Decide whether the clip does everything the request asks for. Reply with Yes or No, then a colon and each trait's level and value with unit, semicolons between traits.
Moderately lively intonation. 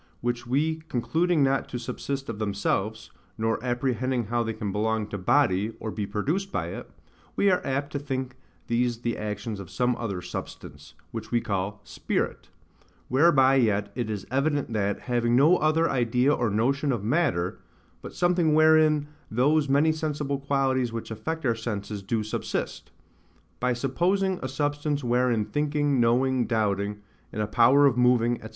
Yes: average, 4.5 semitones